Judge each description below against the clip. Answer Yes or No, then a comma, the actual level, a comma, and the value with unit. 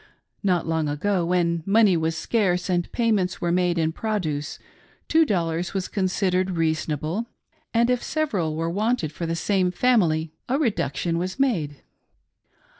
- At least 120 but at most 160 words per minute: Yes, average, 145 wpm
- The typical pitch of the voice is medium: Yes, medium, 180 Hz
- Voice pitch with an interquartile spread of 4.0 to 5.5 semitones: Yes, average, 4.3 semitones